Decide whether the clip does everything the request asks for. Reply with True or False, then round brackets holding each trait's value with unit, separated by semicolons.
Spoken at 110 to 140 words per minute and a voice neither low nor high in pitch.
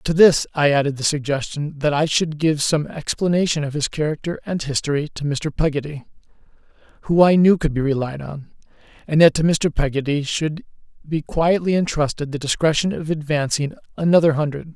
False (170 wpm; 150 Hz)